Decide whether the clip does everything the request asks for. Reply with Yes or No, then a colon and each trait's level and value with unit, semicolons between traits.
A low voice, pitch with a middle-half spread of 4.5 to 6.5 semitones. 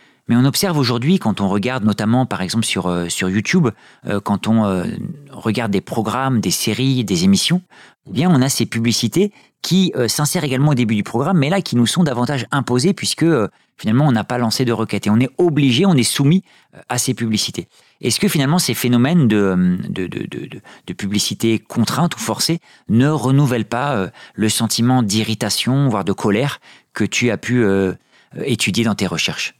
Yes: low, 120 Hz; average, 5.1 semitones